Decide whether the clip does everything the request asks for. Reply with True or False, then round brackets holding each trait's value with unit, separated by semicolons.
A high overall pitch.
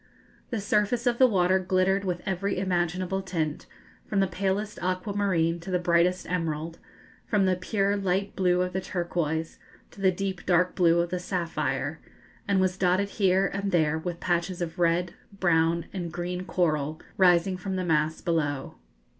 False (180 Hz)